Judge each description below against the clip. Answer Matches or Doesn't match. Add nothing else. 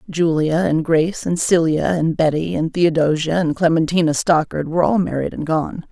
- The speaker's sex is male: Doesn't match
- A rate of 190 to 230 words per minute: Doesn't match